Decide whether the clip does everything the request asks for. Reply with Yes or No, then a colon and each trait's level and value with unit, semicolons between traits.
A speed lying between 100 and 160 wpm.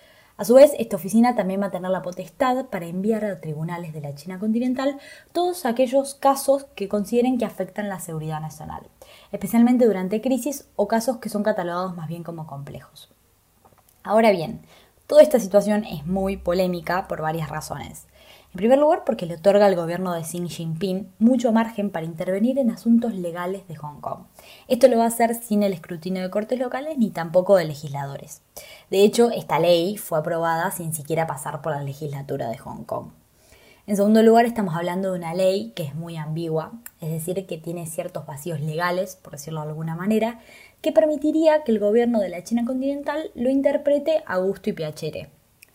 No: average, 185 wpm